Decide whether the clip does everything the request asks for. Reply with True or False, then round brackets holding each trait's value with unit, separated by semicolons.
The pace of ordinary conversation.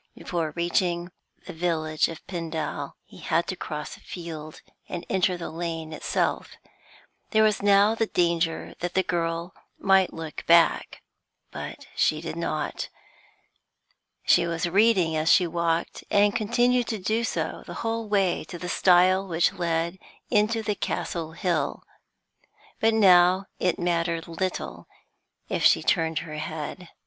True (145 wpm)